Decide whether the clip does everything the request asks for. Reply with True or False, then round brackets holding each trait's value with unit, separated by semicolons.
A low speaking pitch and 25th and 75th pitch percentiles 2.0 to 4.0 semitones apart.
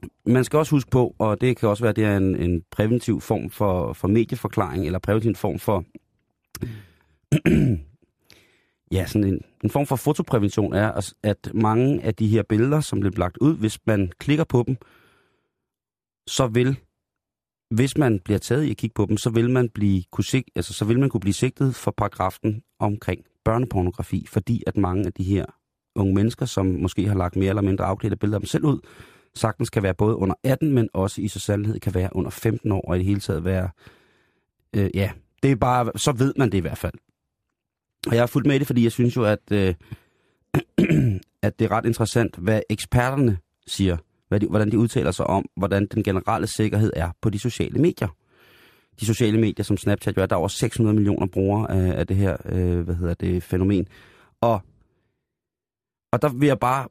True (105 Hz; 3.6 semitones)